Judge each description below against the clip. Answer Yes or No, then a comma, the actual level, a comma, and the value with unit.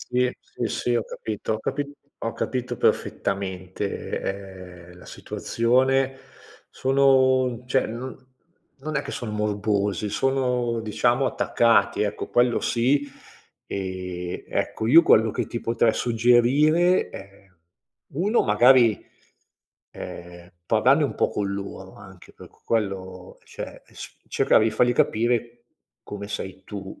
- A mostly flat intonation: No, average, 4.5 semitones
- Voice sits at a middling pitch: No, low, 115 Hz